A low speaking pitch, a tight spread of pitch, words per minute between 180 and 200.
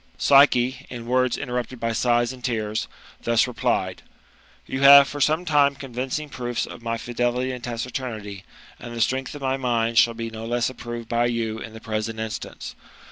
Yes: low, 120 Hz; narrow, 2.1 semitones; average, 190 wpm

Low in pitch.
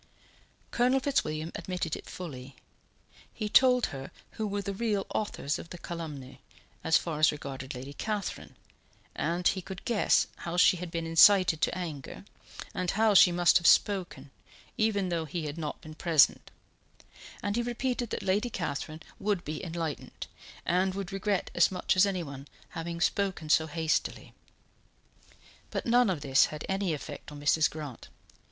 No: medium, 175 Hz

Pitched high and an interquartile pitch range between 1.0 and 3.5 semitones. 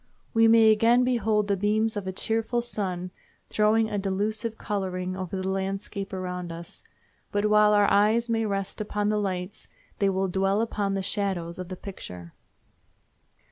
Yes: high, 200 Hz; narrow, 2.4 semitones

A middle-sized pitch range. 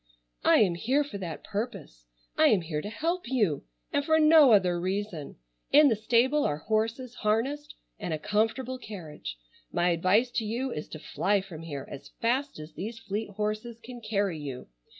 No: wide, 5.9 semitones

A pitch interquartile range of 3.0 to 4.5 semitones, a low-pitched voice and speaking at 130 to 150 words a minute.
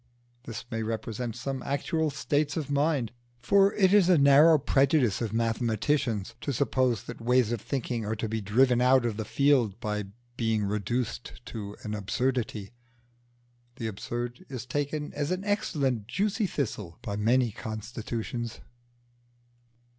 Yes: average, 4.2 semitones; low, 120 Hz; average, 145 wpm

